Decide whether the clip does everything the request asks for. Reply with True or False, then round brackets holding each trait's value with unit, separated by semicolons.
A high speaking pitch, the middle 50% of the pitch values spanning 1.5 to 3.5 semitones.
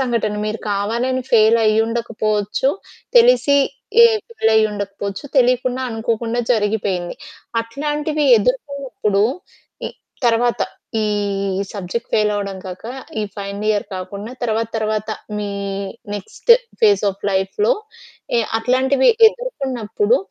False (225 Hz; 3.9 semitones)